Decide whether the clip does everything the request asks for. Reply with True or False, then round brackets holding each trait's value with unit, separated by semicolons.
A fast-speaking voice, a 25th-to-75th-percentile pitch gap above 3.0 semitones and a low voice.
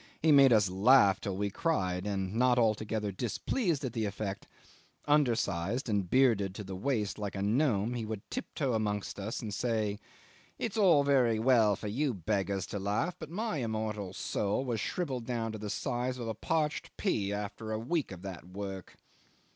False (180 wpm; 4.2 semitones; 110 Hz)